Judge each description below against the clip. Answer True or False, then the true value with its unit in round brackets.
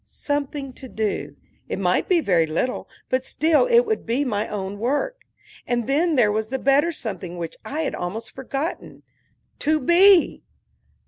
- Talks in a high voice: True (265 Hz)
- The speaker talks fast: False (165 wpm)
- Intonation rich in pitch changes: True (6.5 semitones)